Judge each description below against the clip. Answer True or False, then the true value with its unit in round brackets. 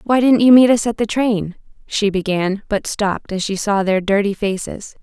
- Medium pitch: False (205 Hz)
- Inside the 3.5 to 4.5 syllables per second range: False (4.9 syllables/s)